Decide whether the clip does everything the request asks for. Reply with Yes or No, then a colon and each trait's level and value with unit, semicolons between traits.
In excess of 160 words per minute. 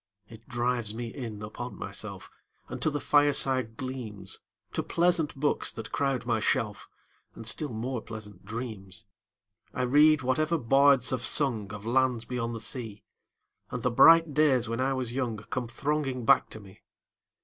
Yes: average, 170 wpm